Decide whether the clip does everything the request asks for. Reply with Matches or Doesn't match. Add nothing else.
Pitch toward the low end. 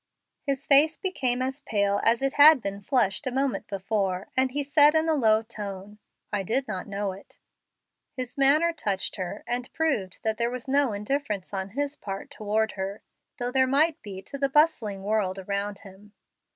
Doesn't match